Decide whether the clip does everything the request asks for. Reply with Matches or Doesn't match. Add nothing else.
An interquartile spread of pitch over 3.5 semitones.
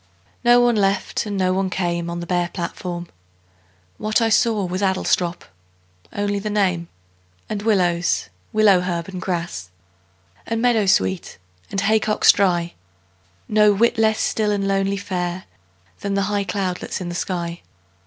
Doesn't match